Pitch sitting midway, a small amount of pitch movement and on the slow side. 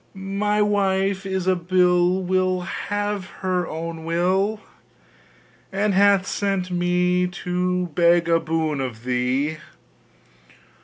Yes: medium, 180 Hz; narrow, 2.2 semitones; slow, 100 wpm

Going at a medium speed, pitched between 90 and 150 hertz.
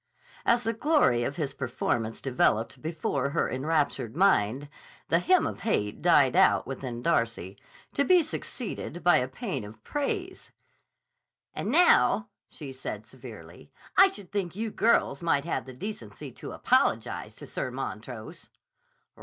No: average, 145 wpm; medium, 160 Hz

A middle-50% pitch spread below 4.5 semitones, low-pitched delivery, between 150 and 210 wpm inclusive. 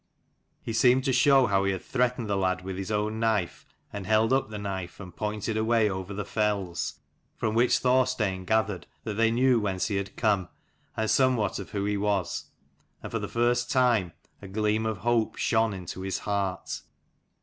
Yes: average, 3.0 semitones; low, 105 Hz; average, 190 wpm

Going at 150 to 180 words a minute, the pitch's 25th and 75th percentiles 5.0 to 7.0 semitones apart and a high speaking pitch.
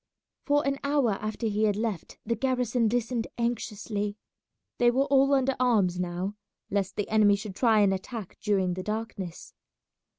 No: average, 160 wpm; average, 3.4 semitones; high, 220 Hz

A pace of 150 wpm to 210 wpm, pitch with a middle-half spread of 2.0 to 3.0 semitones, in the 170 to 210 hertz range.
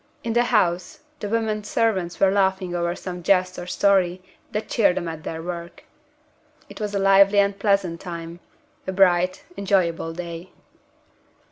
Yes: average, 155 wpm; narrow, 2.4 semitones; medium, 185 Hz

